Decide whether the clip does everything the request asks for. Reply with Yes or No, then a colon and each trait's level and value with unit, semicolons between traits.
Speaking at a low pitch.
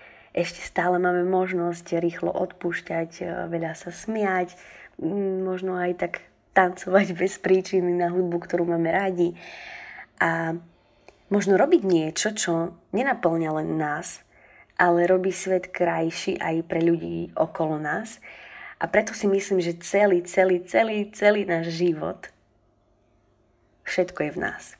No: medium, 175 Hz